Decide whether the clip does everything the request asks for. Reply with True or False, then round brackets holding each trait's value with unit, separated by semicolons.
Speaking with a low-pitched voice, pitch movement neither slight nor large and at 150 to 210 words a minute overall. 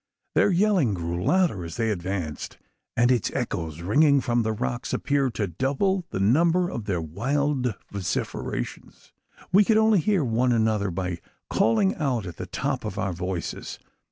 False (115 Hz; 7.8 semitones; 160 wpm)